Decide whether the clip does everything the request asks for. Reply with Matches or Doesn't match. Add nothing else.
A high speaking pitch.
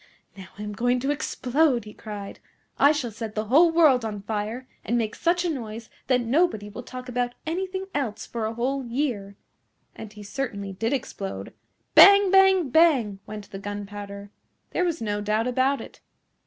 Matches